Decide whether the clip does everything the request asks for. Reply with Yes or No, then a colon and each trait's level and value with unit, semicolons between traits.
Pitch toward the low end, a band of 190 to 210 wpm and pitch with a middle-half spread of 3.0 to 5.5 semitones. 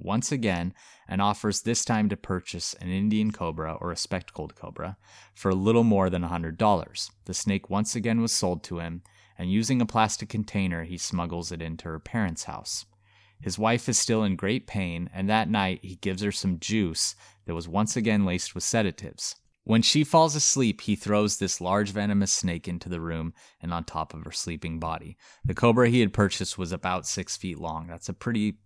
Yes: low, 100 Hz; average, 200 wpm; average, 3.6 semitones